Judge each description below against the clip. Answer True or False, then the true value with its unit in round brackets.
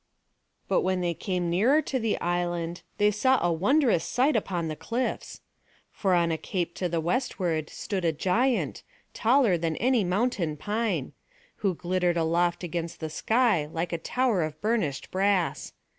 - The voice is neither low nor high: True (180 Hz)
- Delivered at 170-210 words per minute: False (160 wpm)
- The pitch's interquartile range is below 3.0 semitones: False (4.8 semitones)